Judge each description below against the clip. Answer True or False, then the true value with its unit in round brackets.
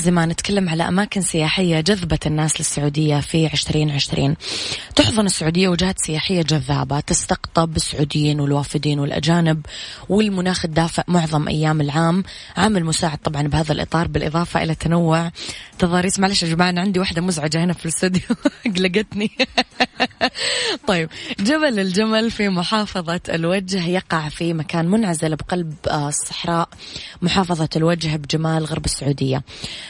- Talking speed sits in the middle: False (120 wpm)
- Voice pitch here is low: False (170 Hz)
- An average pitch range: True (3.2 semitones)